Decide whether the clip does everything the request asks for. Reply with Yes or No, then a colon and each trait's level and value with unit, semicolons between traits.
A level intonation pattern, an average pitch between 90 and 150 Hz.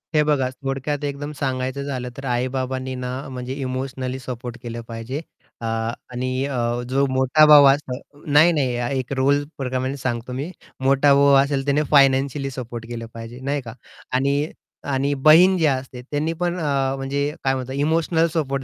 Yes: narrow, 1.9 semitones; low, 135 Hz